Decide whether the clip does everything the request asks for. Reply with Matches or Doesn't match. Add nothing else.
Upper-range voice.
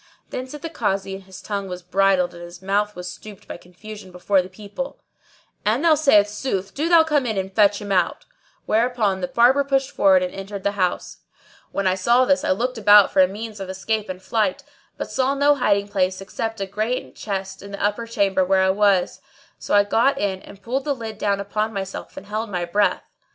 Matches